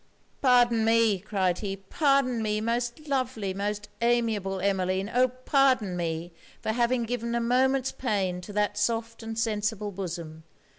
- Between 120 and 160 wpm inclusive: Yes, average, 145 wpm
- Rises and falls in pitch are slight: No, average, 3.7 semitones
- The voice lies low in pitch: No, high, 220 Hz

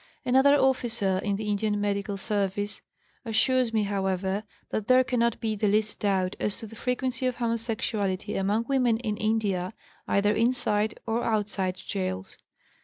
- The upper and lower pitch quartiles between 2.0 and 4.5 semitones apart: Yes, average, 2.7 semitones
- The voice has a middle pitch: No, high, 215 Hz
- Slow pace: No, average, 150 wpm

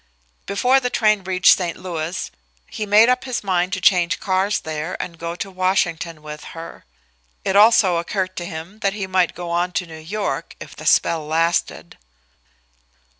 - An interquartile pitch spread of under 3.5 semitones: Yes, average, 2.9 semitones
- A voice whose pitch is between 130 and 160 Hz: No, medium, 185 Hz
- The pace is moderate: Yes, average, 175 wpm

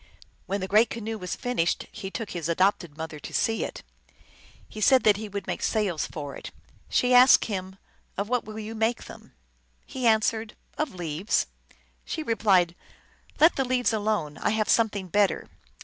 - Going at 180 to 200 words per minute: Yes, average, 195 wpm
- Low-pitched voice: No, high, 210 Hz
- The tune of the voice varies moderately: Yes, average, 3.6 semitones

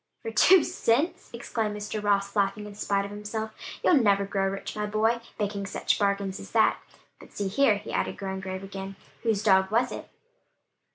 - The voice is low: No, high, 205 Hz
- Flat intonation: Yes, narrow, 1.8 semitones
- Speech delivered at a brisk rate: No, average, 185 wpm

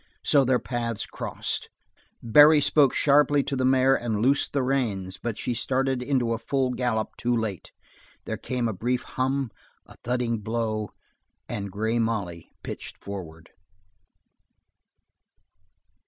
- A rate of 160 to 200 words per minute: No, slow, 135 wpm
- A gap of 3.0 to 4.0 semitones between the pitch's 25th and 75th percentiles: Yes, average, 3.3 semitones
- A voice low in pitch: Yes, low, 120 Hz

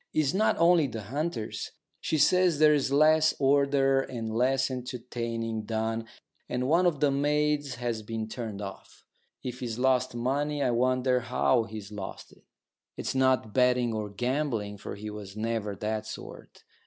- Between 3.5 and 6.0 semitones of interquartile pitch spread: Yes, average, 4.0 semitones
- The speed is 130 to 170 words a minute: Yes, average, 155 wpm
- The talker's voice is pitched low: Yes, low, 125 Hz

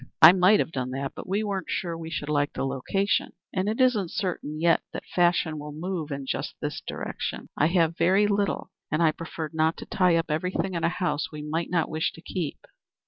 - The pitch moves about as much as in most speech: Yes, average, 3.3 semitones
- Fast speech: Yes, fast, 220 wpm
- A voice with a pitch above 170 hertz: No, medium, 165 Hz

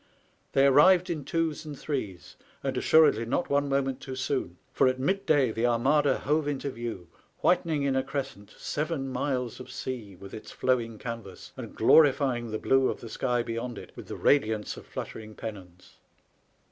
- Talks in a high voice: No, low, 130 Hz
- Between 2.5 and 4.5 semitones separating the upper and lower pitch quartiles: Yes, average, 3.8 semitones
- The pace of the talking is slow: No, average, 170 wpm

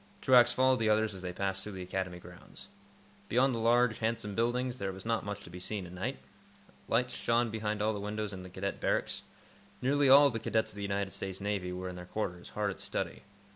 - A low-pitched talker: Yes, low, 105 Hz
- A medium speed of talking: No, fast, 225 wpm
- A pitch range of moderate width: Yes, average, 3.5 semitones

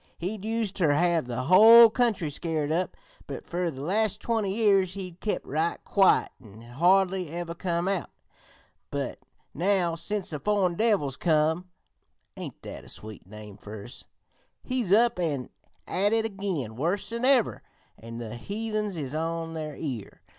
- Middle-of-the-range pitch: Yes, medium, 175 Hz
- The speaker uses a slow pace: No, average, 160 wpm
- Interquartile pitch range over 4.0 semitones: Yes, average, 5.3 semitones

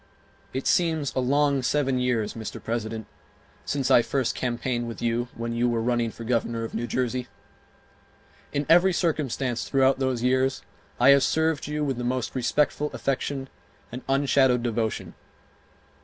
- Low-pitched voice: Yes, low, 130 Hz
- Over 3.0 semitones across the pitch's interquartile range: No, average, 2.7 semitones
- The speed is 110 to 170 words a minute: Yes, average, 155 wpm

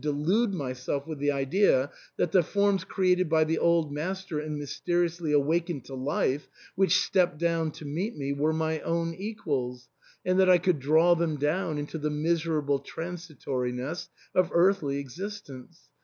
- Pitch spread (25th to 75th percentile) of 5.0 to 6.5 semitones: No, average, 3.6 semitones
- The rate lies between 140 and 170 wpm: Yes, average, 160 wpm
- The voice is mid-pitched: Yes, medium, 160 Hz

